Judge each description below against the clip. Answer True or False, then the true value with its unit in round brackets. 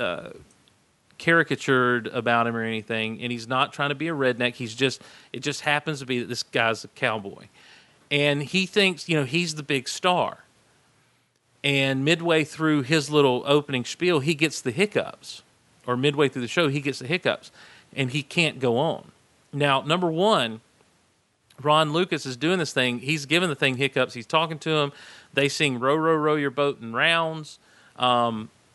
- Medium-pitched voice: True (145 Hz)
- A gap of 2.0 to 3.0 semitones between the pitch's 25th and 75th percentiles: False (4.2 semitones)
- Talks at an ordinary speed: True (185 wpm)